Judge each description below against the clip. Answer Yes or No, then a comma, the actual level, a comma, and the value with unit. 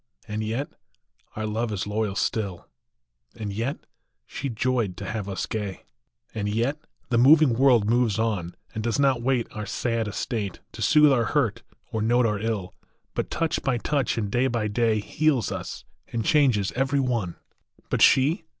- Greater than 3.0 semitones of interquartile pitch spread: Yes, average, 3.7 semitones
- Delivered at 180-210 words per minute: No, average, 170 wpm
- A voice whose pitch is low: Yes, low, 115 Hz